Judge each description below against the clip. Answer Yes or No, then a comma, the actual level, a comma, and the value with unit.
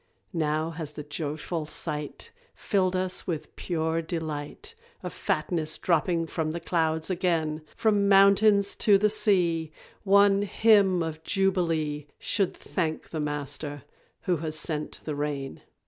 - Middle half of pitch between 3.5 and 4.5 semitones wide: Yes, average, 3.9 semitones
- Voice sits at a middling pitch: Yes, medium, 165 Hz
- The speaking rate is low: Yes, slow, 130 wpm